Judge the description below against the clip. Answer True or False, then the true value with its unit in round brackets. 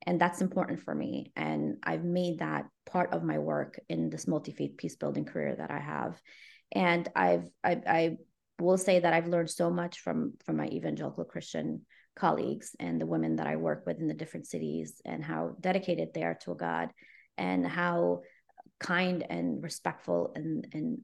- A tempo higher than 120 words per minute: True (185 wpm)